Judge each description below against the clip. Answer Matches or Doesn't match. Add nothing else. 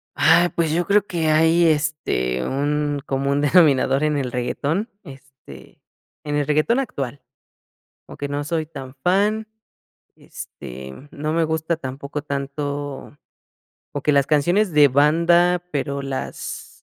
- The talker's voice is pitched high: Doesn't match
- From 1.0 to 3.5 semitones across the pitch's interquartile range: Matches